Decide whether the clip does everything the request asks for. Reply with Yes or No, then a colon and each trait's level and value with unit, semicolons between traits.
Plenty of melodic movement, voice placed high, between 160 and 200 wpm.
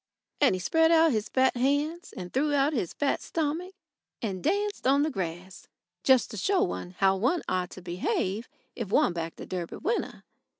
Yes: wide, 9.0 semitones; very high, 260 Hz; average, 185 wpm